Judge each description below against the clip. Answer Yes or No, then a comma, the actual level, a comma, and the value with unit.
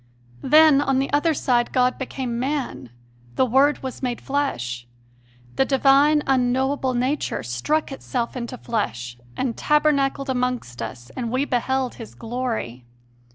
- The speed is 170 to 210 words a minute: No, slow, 135 wpm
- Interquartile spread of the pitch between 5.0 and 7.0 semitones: No, average, 2.7 semitones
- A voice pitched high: Yes, very high, 255 Hz